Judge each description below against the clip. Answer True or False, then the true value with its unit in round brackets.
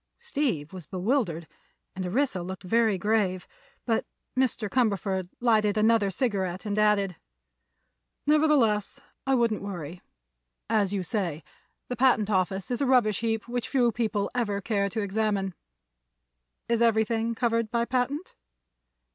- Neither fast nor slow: False (130 wpm)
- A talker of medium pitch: False (215 Hz)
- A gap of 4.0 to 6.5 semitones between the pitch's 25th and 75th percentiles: False (3.6 semitones)